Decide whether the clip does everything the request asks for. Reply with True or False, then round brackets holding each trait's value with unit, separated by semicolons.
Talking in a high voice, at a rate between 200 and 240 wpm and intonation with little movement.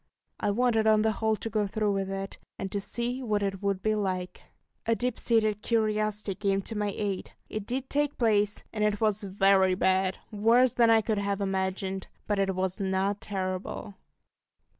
False (205 Hz; 185 wpm; 2.2 semitones)